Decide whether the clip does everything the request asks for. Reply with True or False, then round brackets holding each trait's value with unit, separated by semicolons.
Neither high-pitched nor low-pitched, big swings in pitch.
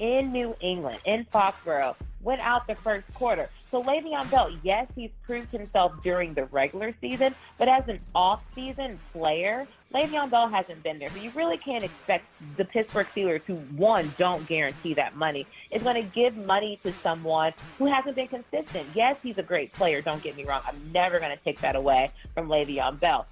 False (200 Hz; 7.2 semitones)